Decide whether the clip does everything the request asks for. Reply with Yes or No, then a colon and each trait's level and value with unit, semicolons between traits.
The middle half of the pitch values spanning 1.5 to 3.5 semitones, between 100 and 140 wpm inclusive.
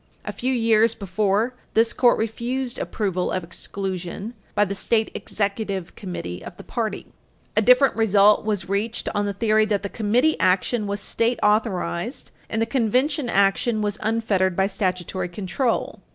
No: average, 2.9 semitones; average, 155 wpm